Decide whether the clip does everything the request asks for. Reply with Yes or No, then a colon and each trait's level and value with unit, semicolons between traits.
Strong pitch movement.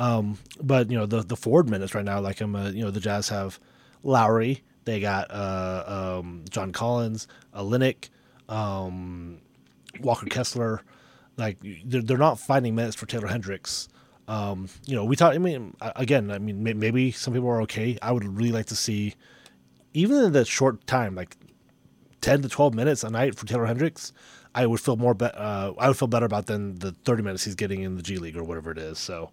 No: average, 3.9 semitones